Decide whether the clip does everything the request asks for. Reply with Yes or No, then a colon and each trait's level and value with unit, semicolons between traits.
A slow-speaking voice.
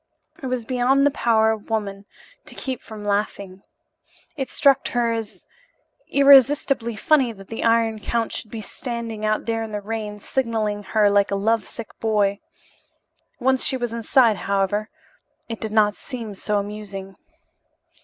No: average, 160 wpm